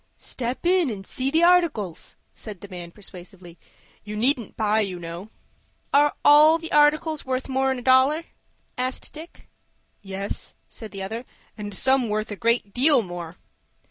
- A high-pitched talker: Yes, high, 235 Hz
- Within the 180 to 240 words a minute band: No, average, 155 wpm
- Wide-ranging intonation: Yes, wide, 6.3 semitones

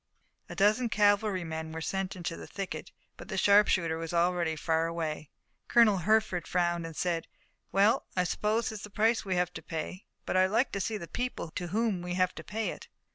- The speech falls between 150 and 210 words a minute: Yes, average, 200 wpm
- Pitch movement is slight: No, average, 3.8 semitones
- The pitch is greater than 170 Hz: Yes, medium, 185 Hz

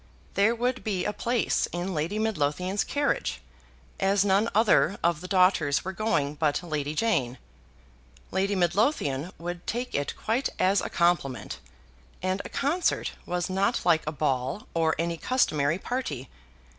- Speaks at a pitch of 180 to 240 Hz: Yes, medium, 185 Hz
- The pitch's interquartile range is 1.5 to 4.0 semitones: No, wide, 5.6 semitones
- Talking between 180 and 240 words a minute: No, average, 145 wpm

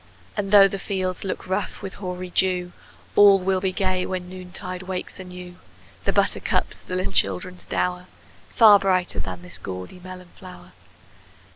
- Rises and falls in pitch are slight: Yes, narrow, 1.0 semitones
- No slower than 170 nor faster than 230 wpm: No, average, 155 wpm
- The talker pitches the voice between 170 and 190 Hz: Yes, medium, 185 Hz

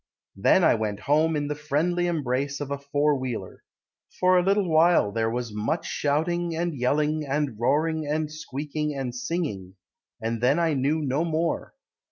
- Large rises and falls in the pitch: No, average, 4.0 semitones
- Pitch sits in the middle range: Yes, medium, 150 Hz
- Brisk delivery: No, average, 170 wpm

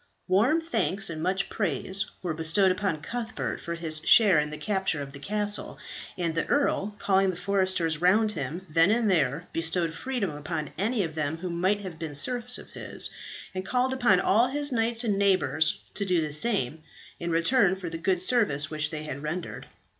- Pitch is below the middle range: No, medium, 185 Hz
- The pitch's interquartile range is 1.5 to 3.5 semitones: No, average, 4.5 semitones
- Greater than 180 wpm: Yes, average, 190 wpm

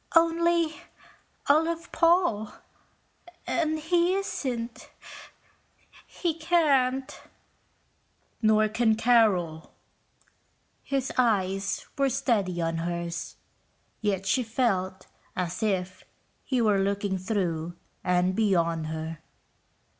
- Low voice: No, high, 215 Hz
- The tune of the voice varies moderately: No, wide, 7.2 semitones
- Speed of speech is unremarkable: No, slow, 90 wpm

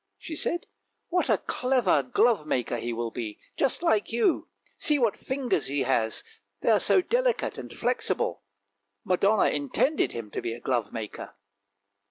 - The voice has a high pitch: Yes, high, 200 Hz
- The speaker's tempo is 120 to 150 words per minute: No, average, 165 wpm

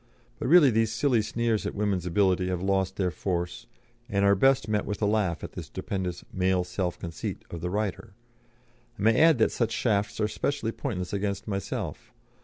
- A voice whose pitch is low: Yes, low, 100 Hz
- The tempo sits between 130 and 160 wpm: No, average, 190 wpm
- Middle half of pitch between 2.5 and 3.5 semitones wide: Yes, average, 3.2 semitones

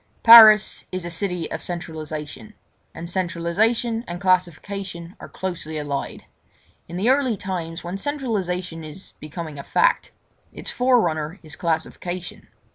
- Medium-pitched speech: Yes, medium, 180 Hz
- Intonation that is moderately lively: Yes, average, 3.7 semitones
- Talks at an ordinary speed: No, slow, 120 wpm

